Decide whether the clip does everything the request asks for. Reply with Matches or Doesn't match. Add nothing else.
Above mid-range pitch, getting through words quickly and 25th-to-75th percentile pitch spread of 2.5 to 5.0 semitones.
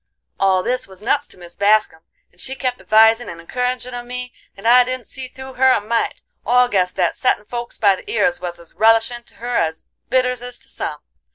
Matches